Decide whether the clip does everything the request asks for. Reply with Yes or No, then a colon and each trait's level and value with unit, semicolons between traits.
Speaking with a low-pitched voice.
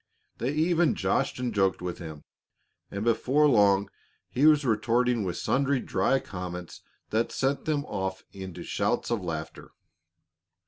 Yes: low, 115 Hz